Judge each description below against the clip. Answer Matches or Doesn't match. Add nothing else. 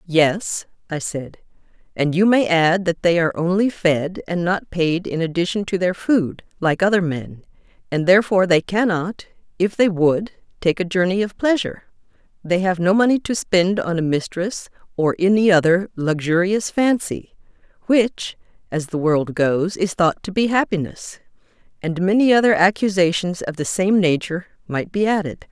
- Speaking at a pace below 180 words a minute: Matches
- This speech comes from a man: Doesn't match